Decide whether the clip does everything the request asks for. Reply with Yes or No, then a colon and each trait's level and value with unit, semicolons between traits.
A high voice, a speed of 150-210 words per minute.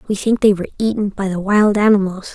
No: high, 200 Hz; fast, 230 wpm